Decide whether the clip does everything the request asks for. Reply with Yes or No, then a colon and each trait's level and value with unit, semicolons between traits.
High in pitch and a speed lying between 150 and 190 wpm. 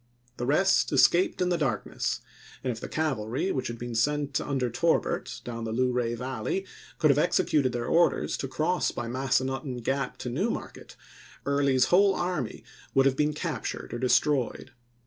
No: low, 135 Hz; average, 165 wpm